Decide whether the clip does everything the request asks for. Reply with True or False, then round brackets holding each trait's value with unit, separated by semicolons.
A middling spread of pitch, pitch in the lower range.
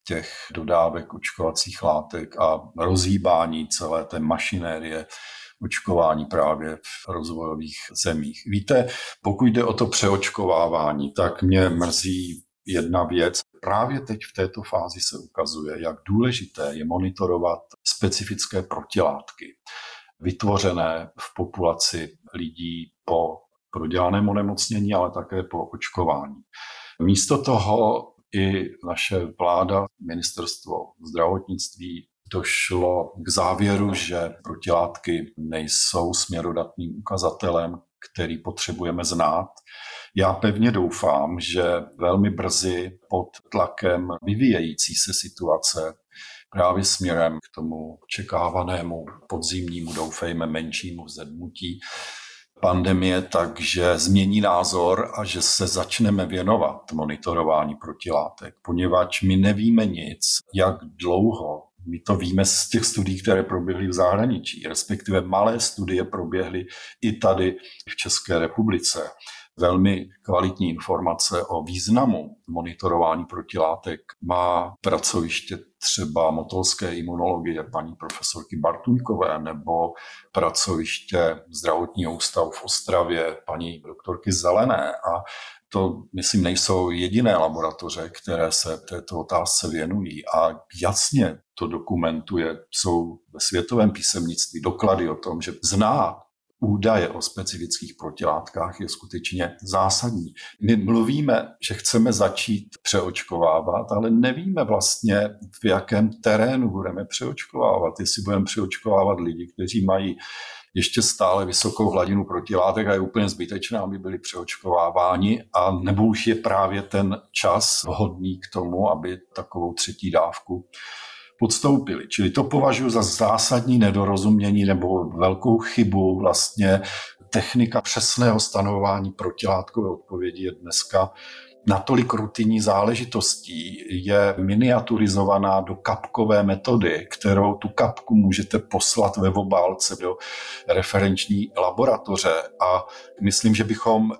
True (3.2 semitones; 95 Hz)